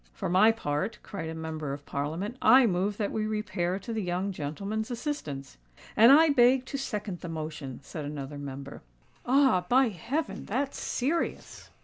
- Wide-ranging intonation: Yes, wide, 7.5 semitones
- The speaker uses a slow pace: No, average, 165 wpm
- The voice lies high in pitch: Yes, high, 195 Hz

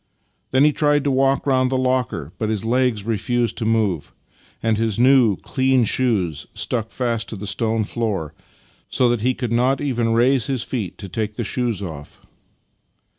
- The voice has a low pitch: Yes, low, 115 Hz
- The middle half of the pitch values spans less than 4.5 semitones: Yes, average, 3.4 semitones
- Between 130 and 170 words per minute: No, average, 180 wpm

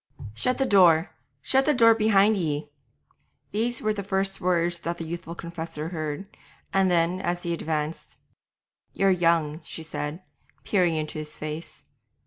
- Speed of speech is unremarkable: Yes, average, 150 wpm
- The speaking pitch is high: No, medium, 175 Hz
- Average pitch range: Yes, average, 3.4 semitones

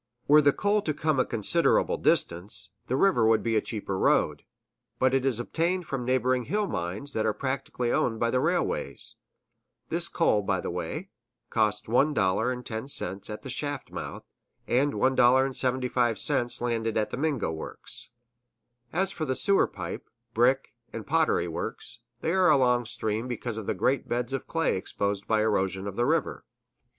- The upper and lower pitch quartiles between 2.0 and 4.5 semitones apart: Yes, average, 4.2 semitones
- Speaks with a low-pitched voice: Yes, low, 125 Hz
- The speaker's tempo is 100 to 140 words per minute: No, average, 165 wpm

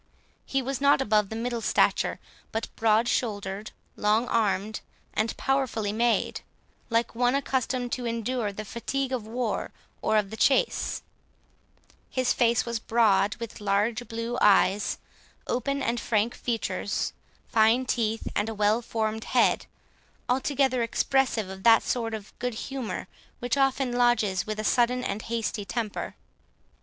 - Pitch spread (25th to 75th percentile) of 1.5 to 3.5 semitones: Yes, narrow, 2.6 semitones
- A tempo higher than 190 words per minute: No, average, 145 wpm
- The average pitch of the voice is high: Yes, high, 230 Hz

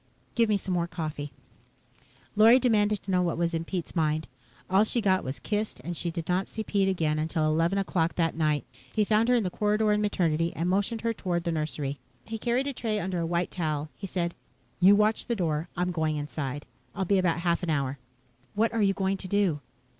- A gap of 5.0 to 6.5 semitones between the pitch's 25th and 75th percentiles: No, average, 4.3 semitones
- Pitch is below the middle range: No, medium, 180 Hz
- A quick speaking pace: Yes, fast, 225 wpm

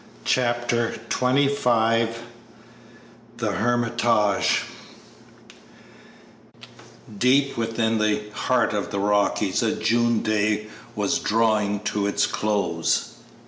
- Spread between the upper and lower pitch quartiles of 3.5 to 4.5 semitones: No, narrow, 2.4 semitones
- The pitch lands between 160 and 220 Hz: No, low, 110 Hz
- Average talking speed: No, slow, 85 wpm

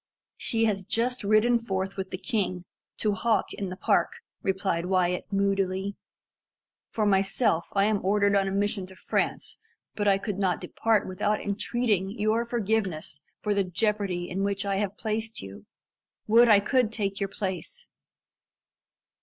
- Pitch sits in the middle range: No, high, 200 Hz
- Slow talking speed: No, average, 155 wpm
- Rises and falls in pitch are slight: Yes, narrow, 2.2 semitones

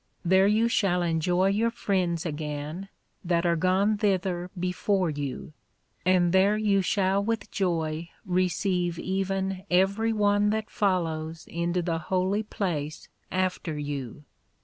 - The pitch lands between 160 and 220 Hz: Yes, medium, 185 Hz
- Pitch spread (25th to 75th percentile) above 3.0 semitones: No, average, 2.7 semitones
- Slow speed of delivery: Yes, slow, 125 wpm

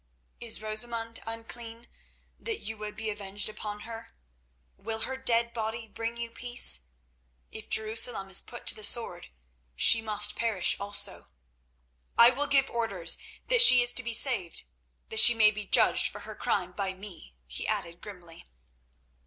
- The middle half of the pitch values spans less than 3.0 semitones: Yes, narrow, 2.6 semitones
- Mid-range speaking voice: No, high, 220 Hz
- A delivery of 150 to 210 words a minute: Yes, average, 155 wpm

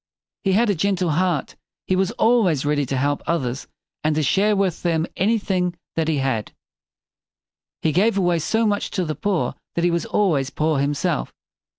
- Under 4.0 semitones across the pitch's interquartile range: No, average, 4.7 semitones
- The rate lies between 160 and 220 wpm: Yes, average, 180 wpm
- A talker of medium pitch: Yes, medium, 170 Hz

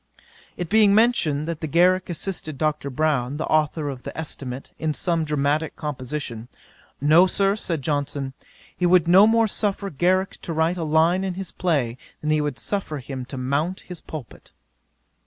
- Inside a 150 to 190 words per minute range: Yes, average, 170 wpm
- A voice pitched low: No, medium, 155 Hz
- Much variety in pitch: No, average, 4.1 semitones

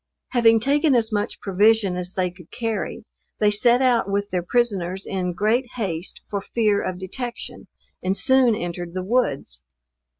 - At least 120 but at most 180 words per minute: Yes, average, 160 wpm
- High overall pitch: Yes, high, 205 Hz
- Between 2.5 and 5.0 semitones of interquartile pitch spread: Yes, average, 4.6 semitones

